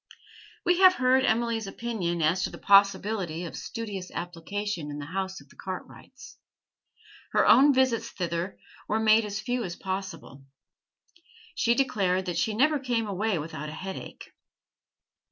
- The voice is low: No, high, 200 Hz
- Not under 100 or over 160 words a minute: Yes, average, 150 wpm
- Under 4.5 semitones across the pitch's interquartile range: No, average, 4.8 semitones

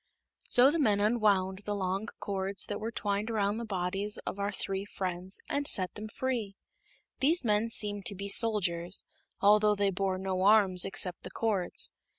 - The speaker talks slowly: No, average, 170 wpm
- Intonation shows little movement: Yes, narrow, 2.1 semitones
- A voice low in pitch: No, high, 200 Hz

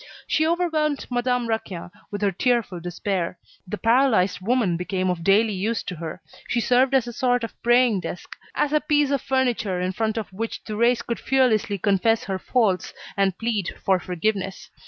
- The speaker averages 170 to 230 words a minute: Yes, average, 180 wpm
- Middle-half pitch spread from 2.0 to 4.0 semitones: No, average, 4.7 semitones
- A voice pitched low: No, high, 220 Hz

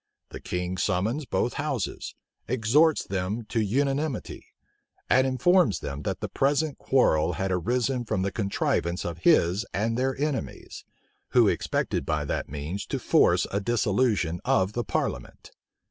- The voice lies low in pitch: Yes, low, 110 Hz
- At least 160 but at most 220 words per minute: No, average, 145 wpm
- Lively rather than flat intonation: Yes, wide, 6.2 semitones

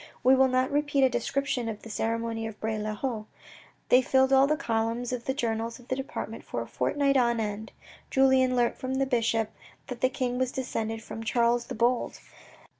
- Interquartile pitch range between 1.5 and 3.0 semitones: Yes, average, 2.7 semitones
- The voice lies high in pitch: Yes, high, 245 Hz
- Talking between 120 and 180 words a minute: No, average, 200 wpm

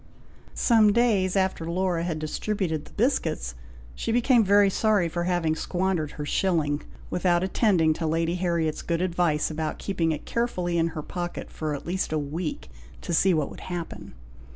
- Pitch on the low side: No, medium, 175 Hz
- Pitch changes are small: No, average, 3.2 semitones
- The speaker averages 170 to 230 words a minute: Yes, average, 175 wpm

